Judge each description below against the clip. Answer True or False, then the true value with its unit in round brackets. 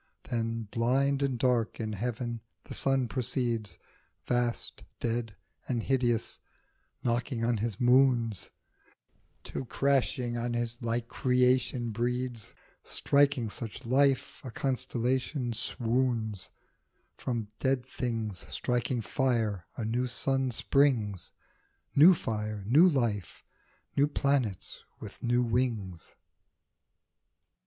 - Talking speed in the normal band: False (105 wpm)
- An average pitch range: False (2.3 semitones)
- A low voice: True (120 Hz)